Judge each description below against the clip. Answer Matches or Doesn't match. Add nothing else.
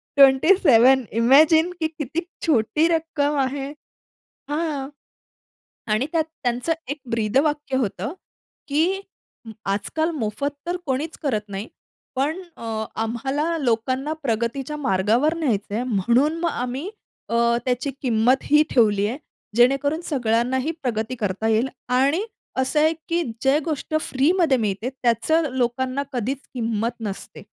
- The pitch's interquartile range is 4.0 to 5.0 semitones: Matches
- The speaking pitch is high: Matches